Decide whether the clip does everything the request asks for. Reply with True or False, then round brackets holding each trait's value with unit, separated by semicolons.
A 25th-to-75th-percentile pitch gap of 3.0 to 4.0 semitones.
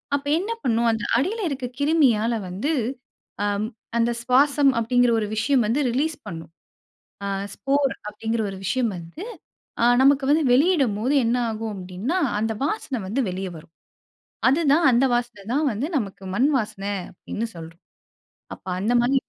False (5.0 semitones)